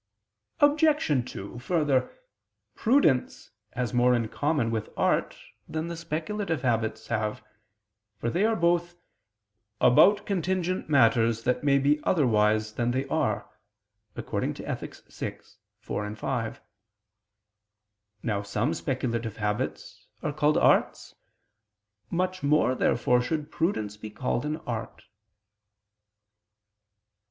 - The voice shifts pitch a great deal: Yes, wide, 6.3 semitones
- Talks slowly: Yes, slow, 110 wpm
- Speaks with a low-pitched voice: Yes, low, 130 Hz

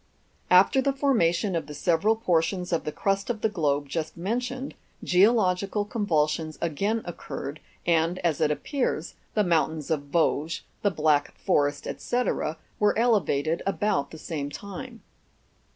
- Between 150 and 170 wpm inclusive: No, average, 140 wpm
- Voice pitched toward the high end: No, medium, 175 Hz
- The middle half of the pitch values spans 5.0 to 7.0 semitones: Yes, average, 5.3 semitones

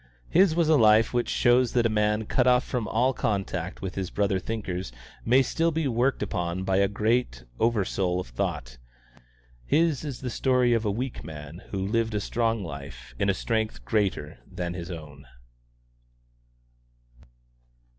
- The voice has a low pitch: Yes, low, 110 Hz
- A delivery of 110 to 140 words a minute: No, average, 165 wpm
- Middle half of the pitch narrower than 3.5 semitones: No, average, 5.0 semitones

